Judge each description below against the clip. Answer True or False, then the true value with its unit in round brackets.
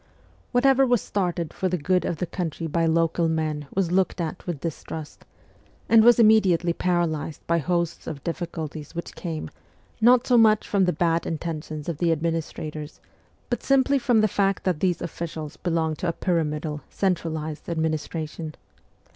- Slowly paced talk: False (165 wpm)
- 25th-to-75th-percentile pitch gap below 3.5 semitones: True (3.1 semitones)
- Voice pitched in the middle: True (170 Hz)